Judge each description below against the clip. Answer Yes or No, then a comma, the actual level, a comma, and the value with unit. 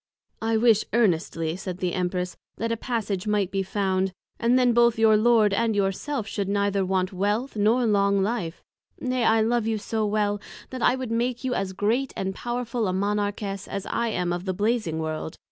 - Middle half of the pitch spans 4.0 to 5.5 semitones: No, average, 3.3 semitones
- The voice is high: Yes, high, 210 Hz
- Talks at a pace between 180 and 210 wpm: Yes, average, 195 wpm